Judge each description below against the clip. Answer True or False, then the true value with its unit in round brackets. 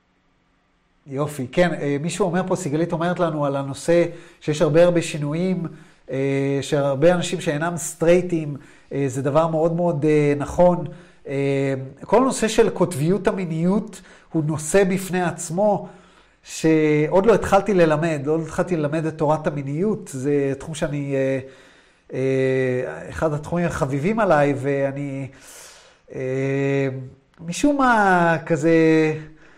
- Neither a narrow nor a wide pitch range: True (4.1 semitones)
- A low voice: False (160 Hz)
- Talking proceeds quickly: False (110 wpm)